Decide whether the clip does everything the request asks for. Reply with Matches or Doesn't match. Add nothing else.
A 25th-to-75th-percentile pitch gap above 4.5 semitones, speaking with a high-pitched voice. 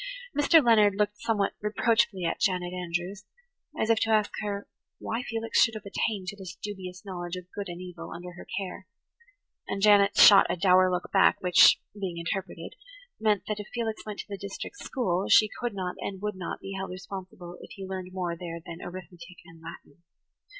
Doesn't match